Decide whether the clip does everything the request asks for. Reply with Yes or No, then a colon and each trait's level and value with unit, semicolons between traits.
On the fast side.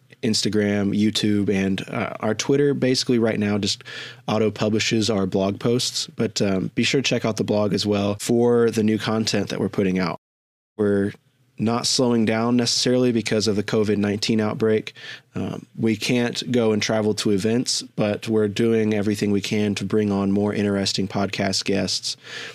No: average, 175 wpm